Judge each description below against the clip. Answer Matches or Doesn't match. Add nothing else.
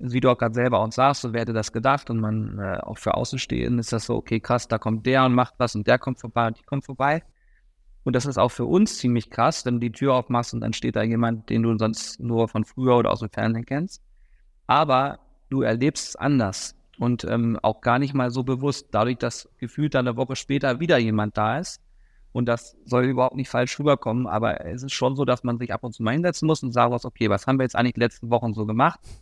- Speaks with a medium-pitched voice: Doesn't match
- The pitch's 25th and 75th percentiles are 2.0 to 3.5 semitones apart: Matches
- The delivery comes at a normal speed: Doesn't match